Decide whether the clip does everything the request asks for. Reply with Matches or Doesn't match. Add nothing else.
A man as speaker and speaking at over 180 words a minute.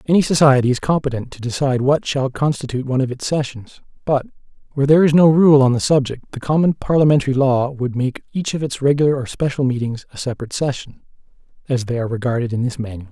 Matches